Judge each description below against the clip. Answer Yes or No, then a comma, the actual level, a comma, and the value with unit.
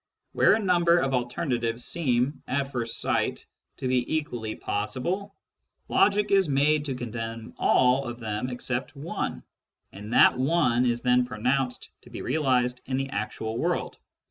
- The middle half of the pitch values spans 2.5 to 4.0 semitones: Yes, average, 3.3 semitones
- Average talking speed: Yes, average, 150 wpm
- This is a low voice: Yes, low, 125 Hz